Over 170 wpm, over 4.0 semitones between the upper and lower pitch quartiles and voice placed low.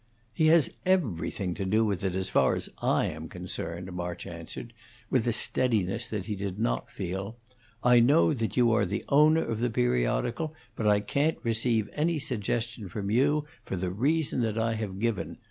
Yes: average, 185 wpm; average, 4.7 semitones; low, 110 Hz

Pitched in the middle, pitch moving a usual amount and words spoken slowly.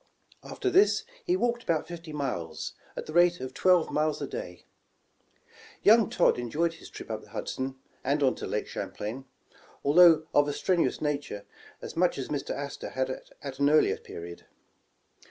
No: medium, 150 Hz; average, 4.6 semitones; average, 170 wpm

